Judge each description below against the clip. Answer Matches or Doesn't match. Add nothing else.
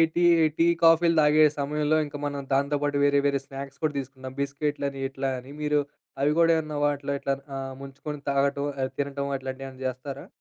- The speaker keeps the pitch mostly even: Matches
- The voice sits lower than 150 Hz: Matches